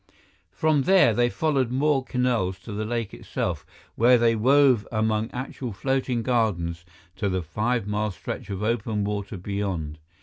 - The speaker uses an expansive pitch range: No, average, 3.8 semitones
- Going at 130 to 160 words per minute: Yes, average, 155 wpm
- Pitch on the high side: No, low, 110 Hz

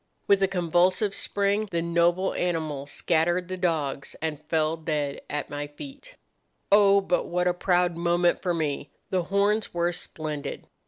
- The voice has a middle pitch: Yes, medium, 175 Hz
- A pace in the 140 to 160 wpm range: Yes, average, 155 wpm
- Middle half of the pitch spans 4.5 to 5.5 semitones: No, average, 3.0 semitones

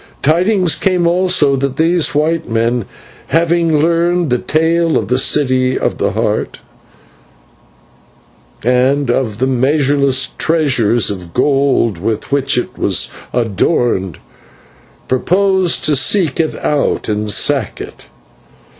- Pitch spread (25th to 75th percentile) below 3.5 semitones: No, average, 5.1 semitones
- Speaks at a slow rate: Yes, slow, 120 wpm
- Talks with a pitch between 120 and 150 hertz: Yes, medium, 140 Hz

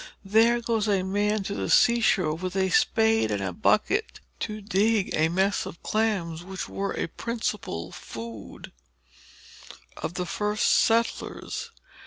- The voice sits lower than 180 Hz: No, high, 200 Hz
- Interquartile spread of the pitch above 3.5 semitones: Yes, average, 4.1 semitones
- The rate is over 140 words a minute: Yes, average, 155 wpm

